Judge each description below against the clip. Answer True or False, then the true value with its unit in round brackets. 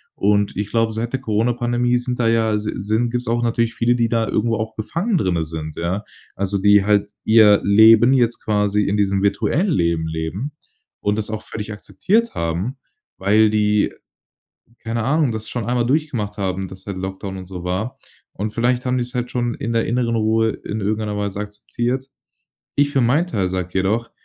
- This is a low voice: True (110 Hz)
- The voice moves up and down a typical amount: True (3.0 semitones)